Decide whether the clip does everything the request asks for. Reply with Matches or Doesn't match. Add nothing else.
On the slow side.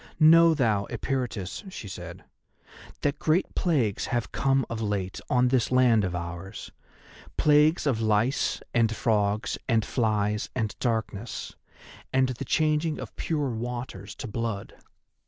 Matches